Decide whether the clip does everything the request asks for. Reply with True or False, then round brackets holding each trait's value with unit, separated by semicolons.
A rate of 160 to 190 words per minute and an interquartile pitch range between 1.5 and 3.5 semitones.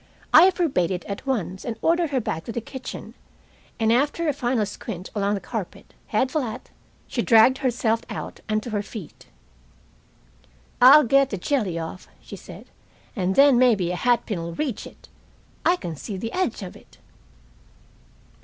False (170 wpm; 5.3 semitones)